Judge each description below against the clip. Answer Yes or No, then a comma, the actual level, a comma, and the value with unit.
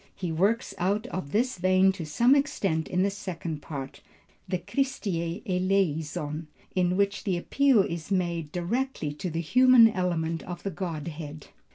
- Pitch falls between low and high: Yes, medium, 180 Hz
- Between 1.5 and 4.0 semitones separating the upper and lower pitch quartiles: Yes, average, 3.7 semitones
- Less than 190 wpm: Yes, average, 155 wpm